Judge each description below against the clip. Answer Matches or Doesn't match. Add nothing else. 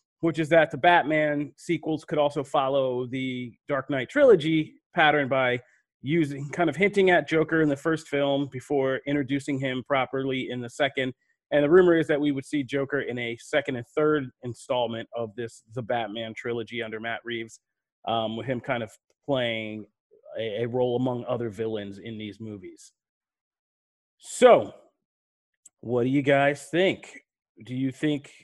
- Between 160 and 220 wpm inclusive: Matches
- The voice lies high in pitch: Doesn't match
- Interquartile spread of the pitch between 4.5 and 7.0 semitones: Doesn't match